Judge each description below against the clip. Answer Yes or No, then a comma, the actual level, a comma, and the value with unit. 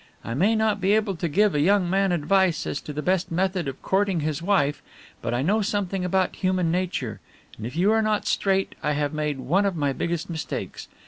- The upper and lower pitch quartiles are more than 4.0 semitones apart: Yes, average, 4.6 semitones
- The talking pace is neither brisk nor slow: No, fast, 220 wpm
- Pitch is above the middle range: No, medium, 180 Hz